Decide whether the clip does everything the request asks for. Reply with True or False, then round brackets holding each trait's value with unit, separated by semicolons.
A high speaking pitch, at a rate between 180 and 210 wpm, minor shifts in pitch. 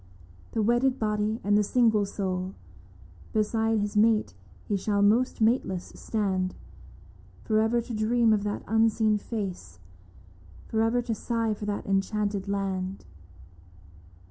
False (210 Hz; 135 wpm; 2.2 semitones)